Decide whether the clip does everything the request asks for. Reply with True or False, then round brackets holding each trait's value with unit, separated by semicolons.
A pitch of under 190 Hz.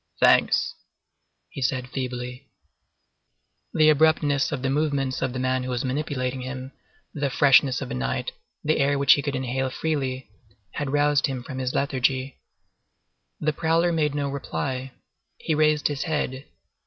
True (135 Hz)